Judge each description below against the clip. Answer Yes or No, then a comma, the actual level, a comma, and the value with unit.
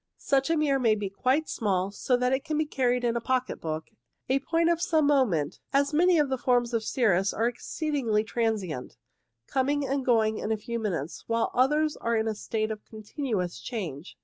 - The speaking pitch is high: Yes, high, 240 Hz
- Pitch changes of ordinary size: Yes, average, 4.5 semitones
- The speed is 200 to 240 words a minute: Yes, fast, 205 wpm